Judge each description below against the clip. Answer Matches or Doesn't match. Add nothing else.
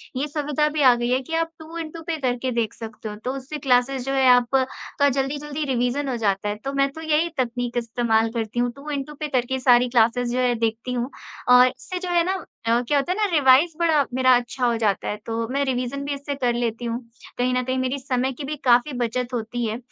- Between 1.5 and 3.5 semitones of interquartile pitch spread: Matches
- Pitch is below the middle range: Doesn't match